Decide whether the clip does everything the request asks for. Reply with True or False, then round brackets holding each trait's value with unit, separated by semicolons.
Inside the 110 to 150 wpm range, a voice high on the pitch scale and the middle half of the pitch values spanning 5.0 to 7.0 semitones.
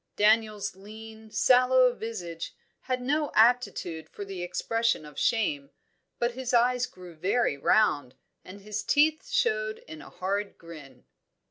True (135 wpm; 215 Hz; 5.4 semitones)